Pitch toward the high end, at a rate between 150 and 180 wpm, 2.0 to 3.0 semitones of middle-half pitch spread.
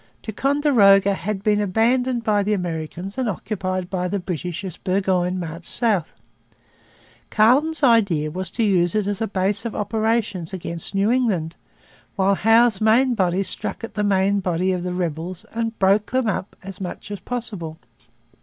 No: high, 200 Hz; average, 165 wpm; average, 3.5 semitones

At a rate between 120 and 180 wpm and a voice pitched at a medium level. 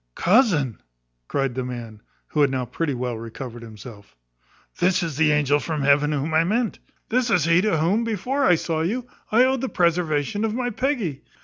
No: average, 190 wpm; medium, 160 Hz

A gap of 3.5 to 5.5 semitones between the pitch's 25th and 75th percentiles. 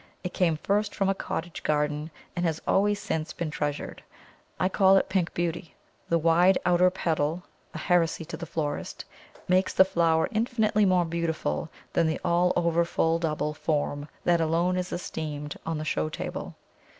No: narrow, 2.5 semitones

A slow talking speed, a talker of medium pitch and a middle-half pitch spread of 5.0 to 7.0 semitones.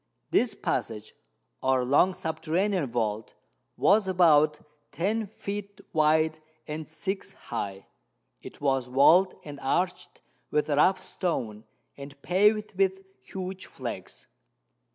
Yes: slow, 110 wpm; medium, 160 Hz; wide, 5.5 semitones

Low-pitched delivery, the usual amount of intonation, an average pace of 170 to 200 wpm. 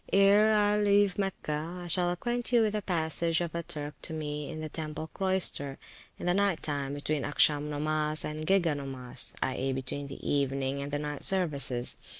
No: medium, 155 Hz; average, 4.6 semitones; average, 185 wpm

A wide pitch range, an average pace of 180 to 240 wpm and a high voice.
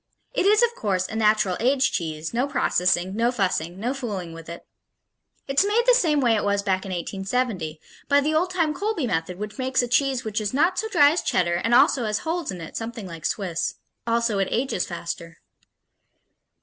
Yes: wide, 7.2 semitones; average, 200 wpm; high, 225 Hz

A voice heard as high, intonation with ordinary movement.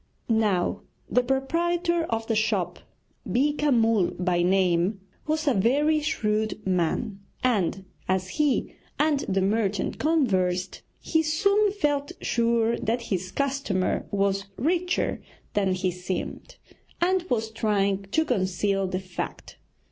No: high, 220 Hz; wide, 7.5 semitones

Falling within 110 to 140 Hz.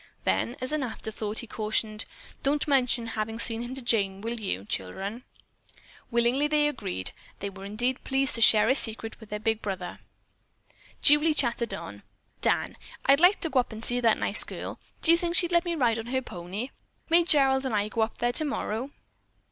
No: high, 235 Hz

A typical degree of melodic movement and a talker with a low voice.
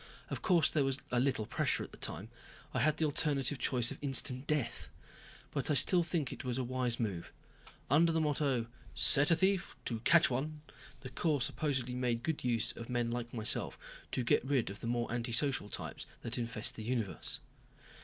Yes: average, 3.8 semitones; low, 130 Hz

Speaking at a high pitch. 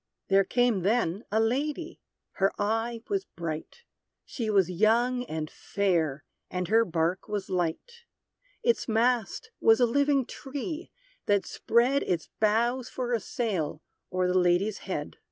Yes: high, 220 Hz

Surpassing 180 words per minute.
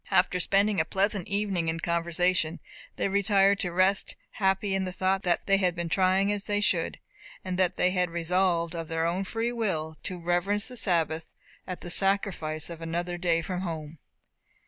Yes: average, 190 wpm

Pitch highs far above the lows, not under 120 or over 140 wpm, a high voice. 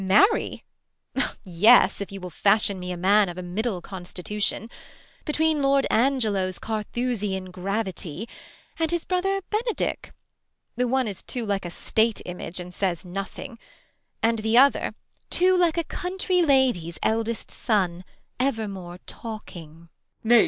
Yes: wide, 6.2 semitones; slow, 135 wpm; high, 215 Hz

